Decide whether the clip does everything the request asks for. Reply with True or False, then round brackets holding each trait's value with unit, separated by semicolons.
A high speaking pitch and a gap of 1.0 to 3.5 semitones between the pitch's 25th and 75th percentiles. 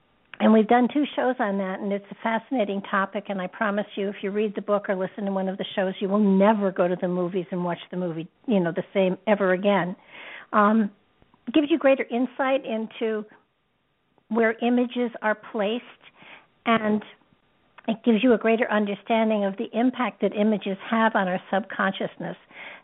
True (210 Hz; 3.1 semitones)